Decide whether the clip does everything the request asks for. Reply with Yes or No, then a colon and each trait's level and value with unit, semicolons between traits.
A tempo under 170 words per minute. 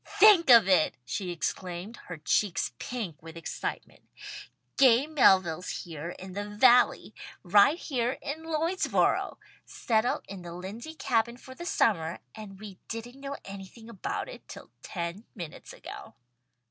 Yes: average, 140 wpm